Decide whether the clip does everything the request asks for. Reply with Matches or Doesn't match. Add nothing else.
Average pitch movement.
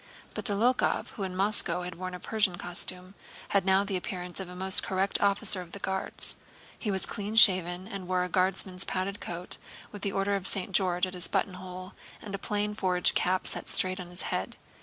Doesn't match